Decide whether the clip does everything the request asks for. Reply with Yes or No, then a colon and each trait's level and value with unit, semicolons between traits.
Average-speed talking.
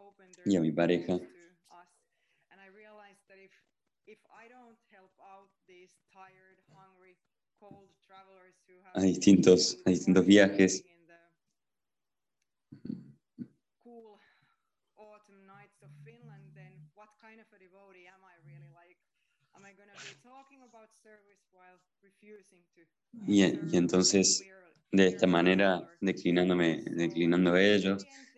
No: slow, 40 wpm